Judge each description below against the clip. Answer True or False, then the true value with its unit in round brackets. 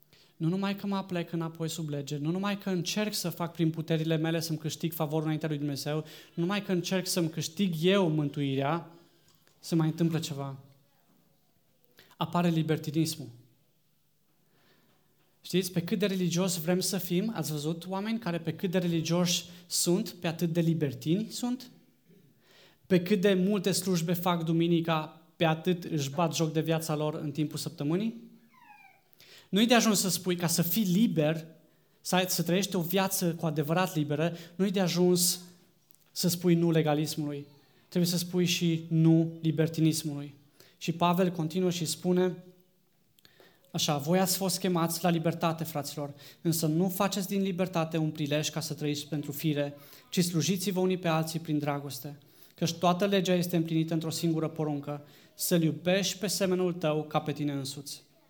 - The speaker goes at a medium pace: True (160 wpm)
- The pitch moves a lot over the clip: False (2.7 semitones)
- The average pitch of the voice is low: False (170 Hz)